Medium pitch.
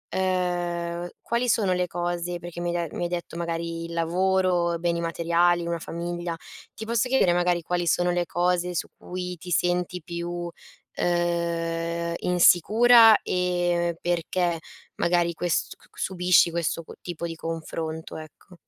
Yes: medium, 175 Hz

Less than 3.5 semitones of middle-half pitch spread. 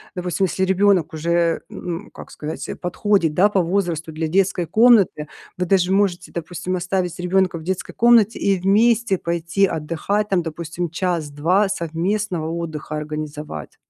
Yes: average, 3.1 semitones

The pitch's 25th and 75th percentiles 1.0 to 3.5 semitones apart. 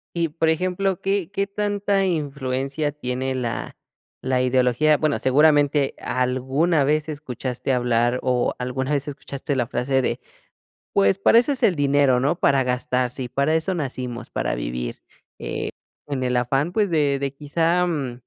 No: average, 3.9 semitones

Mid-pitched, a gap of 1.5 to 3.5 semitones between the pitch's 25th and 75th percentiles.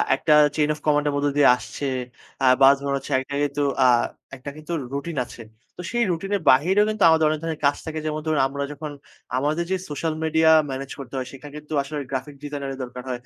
Yes: medium, 145 Hz; narrow, 2.4 semitones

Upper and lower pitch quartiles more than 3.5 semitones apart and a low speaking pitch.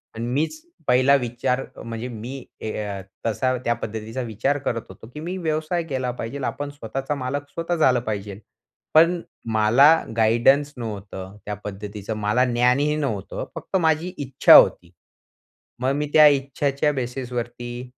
Yes: average, 4.3 semitones; low, 125 Hz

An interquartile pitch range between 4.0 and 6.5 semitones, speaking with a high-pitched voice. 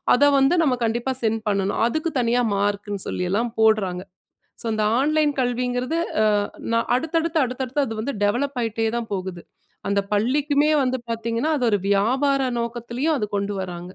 Yes: average, 4.7 semitones; high, 235 Hz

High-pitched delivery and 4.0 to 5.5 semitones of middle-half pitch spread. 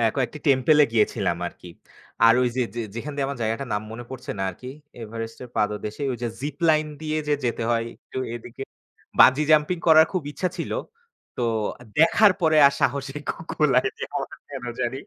No: low, 130 Hz; average, 4.4 semitones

